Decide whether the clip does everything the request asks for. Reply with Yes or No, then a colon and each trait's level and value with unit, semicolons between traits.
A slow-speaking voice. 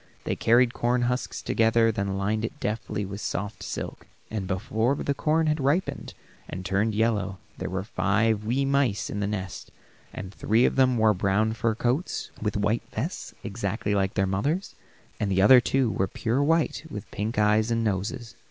No: average, 185 wpm